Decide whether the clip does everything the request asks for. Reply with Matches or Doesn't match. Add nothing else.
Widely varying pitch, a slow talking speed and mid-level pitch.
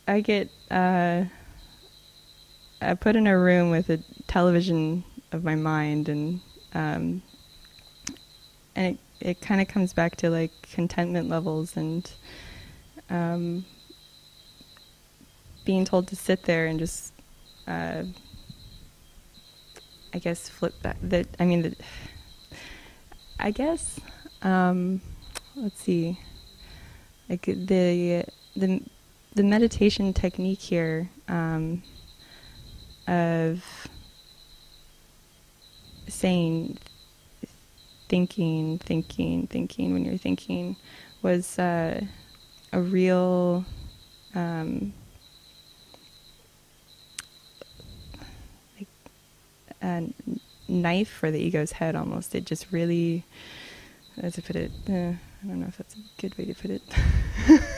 Doesn't match